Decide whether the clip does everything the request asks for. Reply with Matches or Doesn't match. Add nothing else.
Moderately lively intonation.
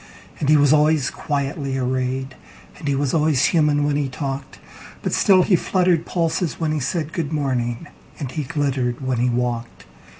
Matches